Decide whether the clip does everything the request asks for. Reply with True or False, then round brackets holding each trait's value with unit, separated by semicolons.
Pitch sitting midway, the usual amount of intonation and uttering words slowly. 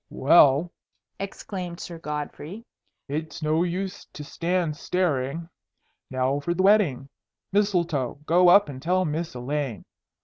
True (165 Hz; 4.1 semitones; 125 wpm)